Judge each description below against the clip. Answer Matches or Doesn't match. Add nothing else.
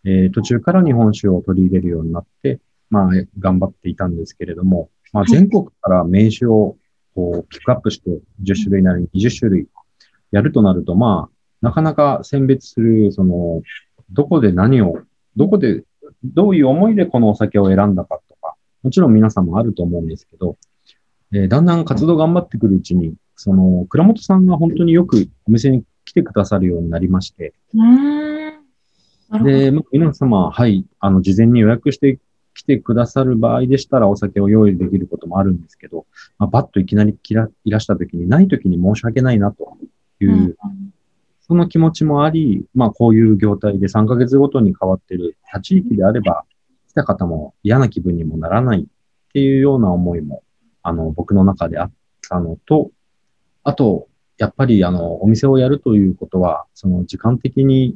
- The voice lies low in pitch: Matches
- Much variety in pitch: Matches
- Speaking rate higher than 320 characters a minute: Matches